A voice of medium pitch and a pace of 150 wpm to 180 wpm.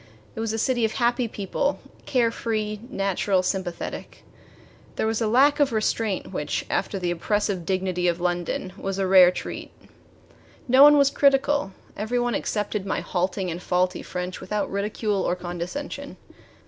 No: high, 205 Hz; average, 160 wpm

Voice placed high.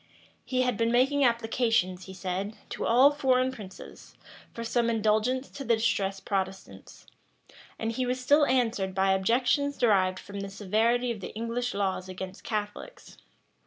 Yes: high, 225 Hz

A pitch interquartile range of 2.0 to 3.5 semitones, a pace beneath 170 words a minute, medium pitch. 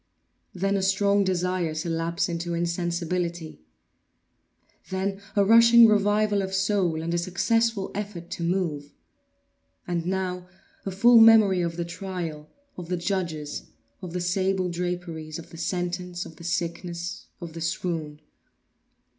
Yes: narrow, 2.4 semitones; average, 140 wpm; medium, 180 Hz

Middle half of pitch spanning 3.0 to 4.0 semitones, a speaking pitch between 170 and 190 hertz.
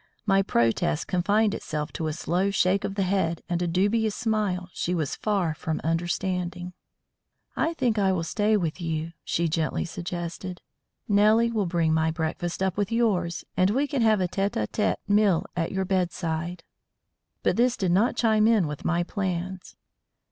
Yes: average, 3.5 semitones; medium, 185 Hz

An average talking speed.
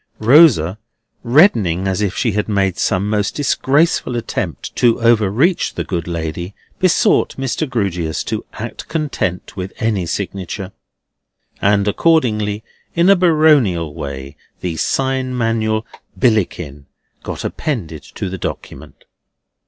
No: slow, 120 wpm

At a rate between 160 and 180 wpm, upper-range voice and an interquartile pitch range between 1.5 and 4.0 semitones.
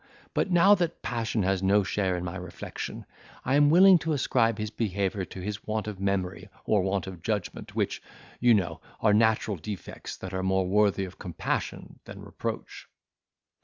No: average, 175 wpm; low, 100 Hz; average, 3.1 semitones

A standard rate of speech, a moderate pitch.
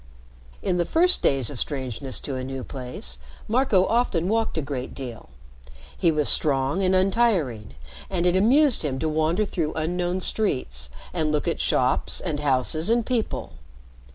Yes: average, 160 wpm; medium, 160 Hz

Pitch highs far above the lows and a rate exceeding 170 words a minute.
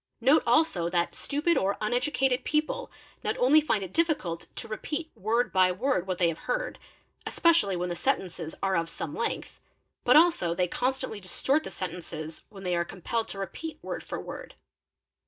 Yes: wide, 8.3 semitones; average, 180 wpm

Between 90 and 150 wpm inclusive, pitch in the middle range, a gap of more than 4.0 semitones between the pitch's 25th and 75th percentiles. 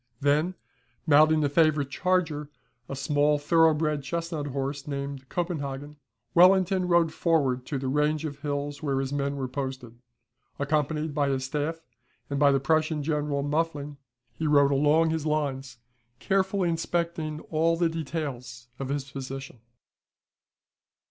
No: average, 140 wpm; medium, 150 Hz; narrow, 2.6 semitones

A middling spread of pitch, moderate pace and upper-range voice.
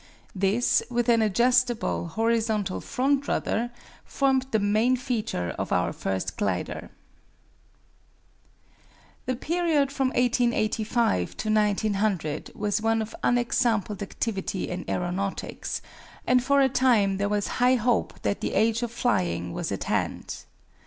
No: average, 3.6 semitones; slow, 125 wpm; high, 225 Hz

